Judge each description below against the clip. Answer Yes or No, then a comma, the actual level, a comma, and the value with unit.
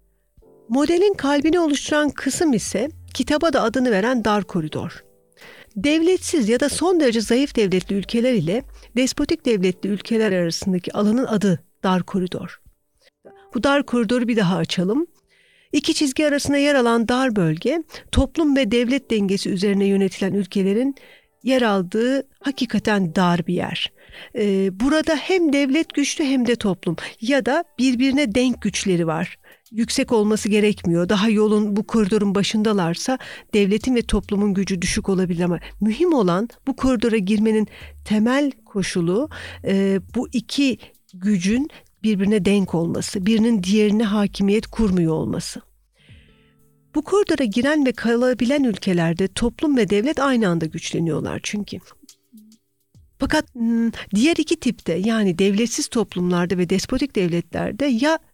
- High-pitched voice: Yes, high, 225 Hz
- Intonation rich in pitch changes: Yes, wide, 5.7 semitones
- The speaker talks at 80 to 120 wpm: No, average, 130 wpm